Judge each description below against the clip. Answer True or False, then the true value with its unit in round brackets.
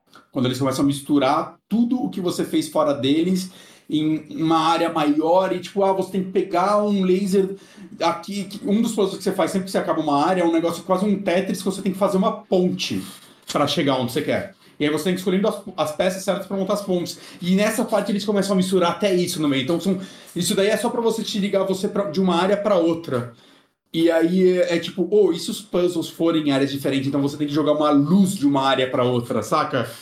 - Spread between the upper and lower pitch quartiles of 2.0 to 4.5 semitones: True (3.8 semitones)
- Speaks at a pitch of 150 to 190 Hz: True (185 Hz)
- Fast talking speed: True (250 wpm)